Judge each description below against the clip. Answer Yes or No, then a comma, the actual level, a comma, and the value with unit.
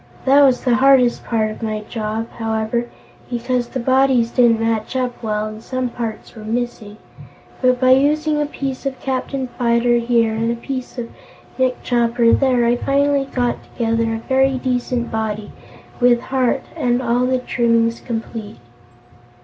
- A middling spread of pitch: No, narrow, 2.2 semitones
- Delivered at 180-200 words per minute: No, average, 160 wpm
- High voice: Yes, high, 240 Hz